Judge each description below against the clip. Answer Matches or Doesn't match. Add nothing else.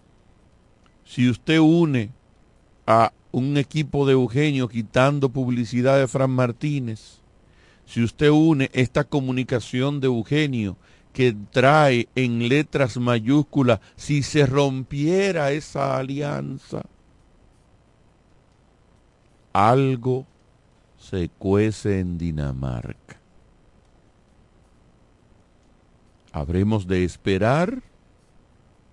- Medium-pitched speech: Doesn't match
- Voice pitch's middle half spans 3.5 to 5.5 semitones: Matches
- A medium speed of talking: Doesn't match